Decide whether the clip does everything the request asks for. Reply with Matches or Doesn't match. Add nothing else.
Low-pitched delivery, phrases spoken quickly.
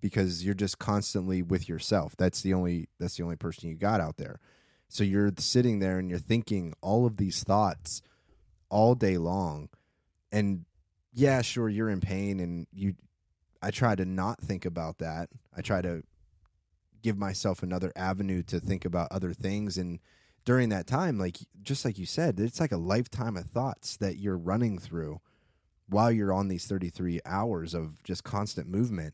Doesn't match